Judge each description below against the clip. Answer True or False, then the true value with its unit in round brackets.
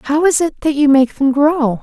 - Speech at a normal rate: False (265 wpm)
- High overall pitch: True (290 Hz)